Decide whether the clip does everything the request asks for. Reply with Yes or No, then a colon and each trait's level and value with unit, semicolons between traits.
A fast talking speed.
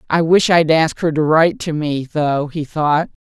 Yes: fast, 220 wpm